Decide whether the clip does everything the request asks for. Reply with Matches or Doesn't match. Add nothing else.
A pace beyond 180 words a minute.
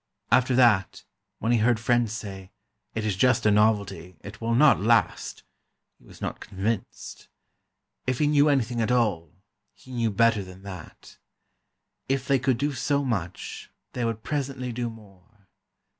Doesn't match